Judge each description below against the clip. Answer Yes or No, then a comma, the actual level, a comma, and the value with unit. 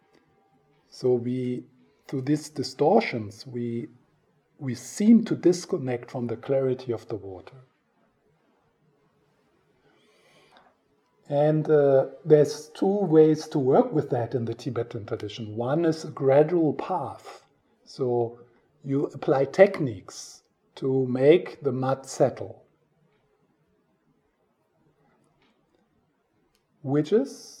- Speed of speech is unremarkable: No, slow, 100 wpm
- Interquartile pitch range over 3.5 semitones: Yes, average, 3.9 semitones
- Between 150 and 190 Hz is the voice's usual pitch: No, low, 135 Hz